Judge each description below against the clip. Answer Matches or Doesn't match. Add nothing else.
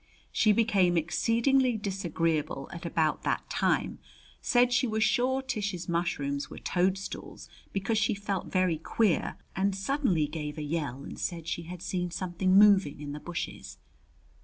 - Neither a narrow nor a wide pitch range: Matches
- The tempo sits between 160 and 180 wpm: Doesn't match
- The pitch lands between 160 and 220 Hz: Matches